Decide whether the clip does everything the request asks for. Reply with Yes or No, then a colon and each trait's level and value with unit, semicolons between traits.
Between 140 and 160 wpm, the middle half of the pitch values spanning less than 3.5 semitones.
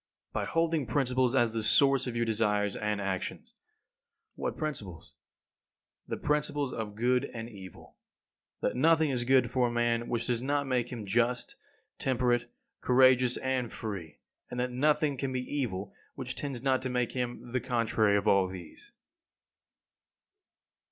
Yes: average, 150 wpm; average, 2.8 semitones